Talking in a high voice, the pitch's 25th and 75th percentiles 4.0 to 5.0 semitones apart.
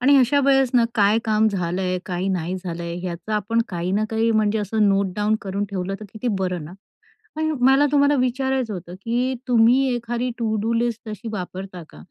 Yes: high, 215 Hz; average, 4.5 semitones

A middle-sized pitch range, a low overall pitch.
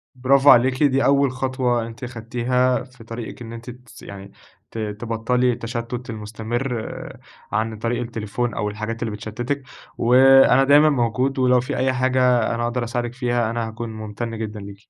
No: narrow, 2.2 semitones; low, 120 Hz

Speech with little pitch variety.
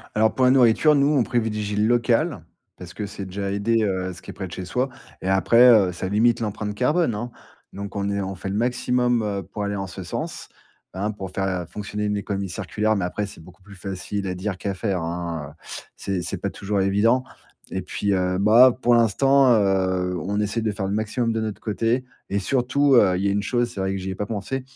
No: average, 3.2 semitones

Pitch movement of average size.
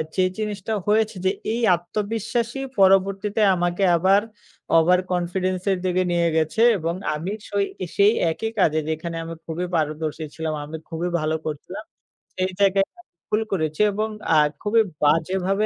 Yes: average, 3.8 semitones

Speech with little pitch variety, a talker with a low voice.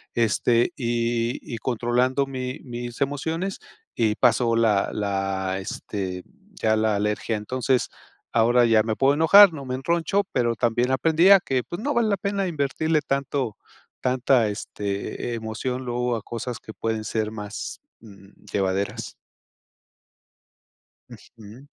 No: average, 3.8 semitones; low, 120 Hz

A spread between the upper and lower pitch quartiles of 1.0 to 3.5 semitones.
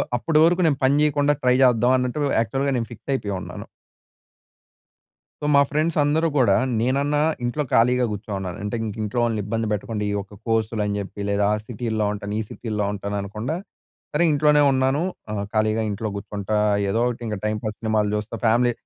No: average, 4.1 semitones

